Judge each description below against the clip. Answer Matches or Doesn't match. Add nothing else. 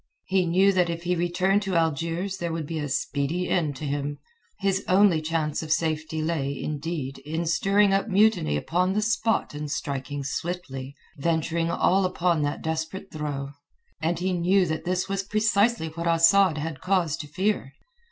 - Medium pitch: Matches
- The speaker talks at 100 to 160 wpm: Doesn't match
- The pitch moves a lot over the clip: Doesn't match